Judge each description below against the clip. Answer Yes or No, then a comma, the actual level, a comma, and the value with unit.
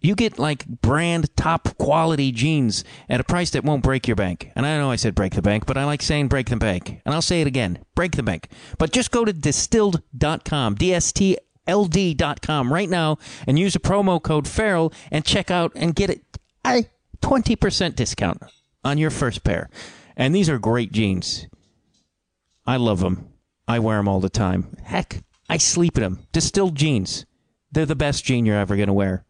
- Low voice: No, medium, 145 Hz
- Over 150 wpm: Yes, average, 195 wpm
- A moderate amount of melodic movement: No, wide, 7.1 semitones